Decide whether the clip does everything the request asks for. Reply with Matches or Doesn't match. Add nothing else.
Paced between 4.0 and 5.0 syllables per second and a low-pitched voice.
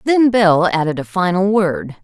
Doesn't match